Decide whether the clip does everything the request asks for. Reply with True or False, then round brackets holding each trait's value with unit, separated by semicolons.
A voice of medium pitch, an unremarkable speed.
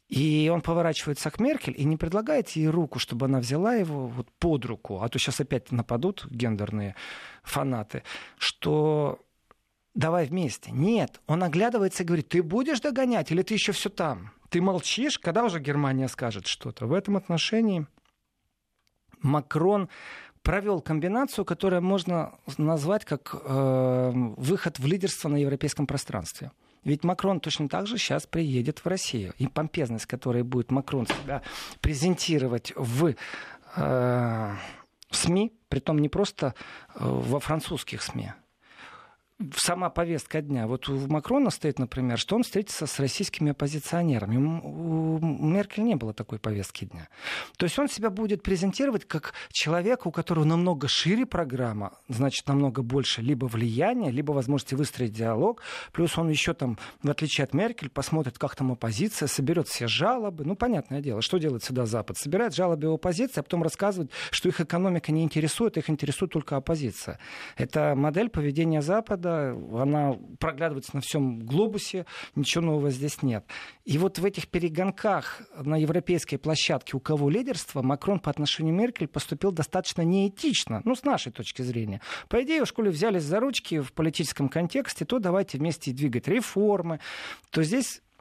True (155 Hz; 150 wpm)